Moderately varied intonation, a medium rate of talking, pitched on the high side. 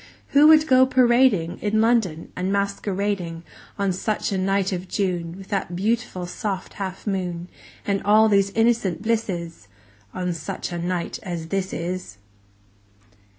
Yes: average, 3.4 semitones; average, 150 wpm; high, 195 Hz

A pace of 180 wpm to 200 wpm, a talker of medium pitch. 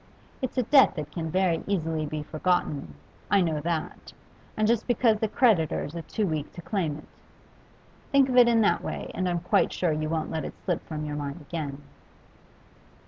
Yes: average, 195 wpm; medium, 170 Hz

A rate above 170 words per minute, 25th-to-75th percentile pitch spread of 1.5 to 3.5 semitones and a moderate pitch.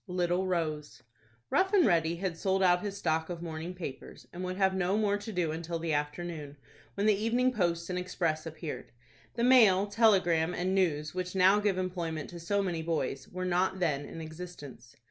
Yes: average, 190 wpm; average, 2.9 semitones; medium, 180 Hz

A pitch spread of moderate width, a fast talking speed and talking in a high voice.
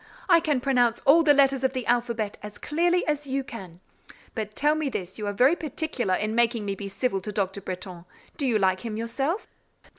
No: wide, 5.7 semitones; fast, 210 wpm; high, 235 Hz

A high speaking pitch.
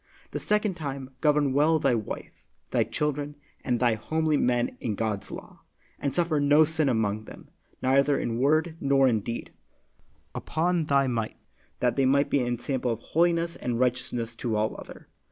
No: low, 135 Hz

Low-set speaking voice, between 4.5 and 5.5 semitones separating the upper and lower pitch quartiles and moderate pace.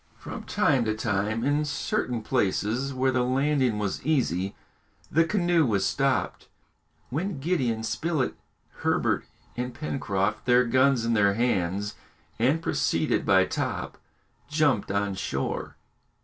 No: low, 125 Hz; average, 5.2 semitones; slow, 125 wpm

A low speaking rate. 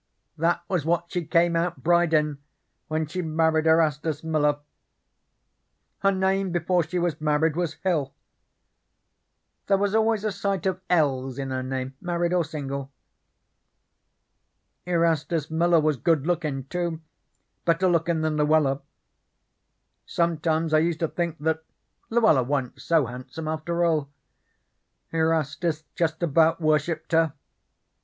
Yes: slow, 130 wpm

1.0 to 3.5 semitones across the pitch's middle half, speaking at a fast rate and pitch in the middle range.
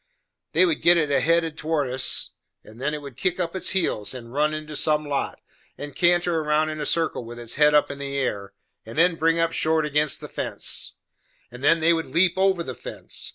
Yes: average, 3.1 semitones; fast, 220 wpm; medium, 155 Hz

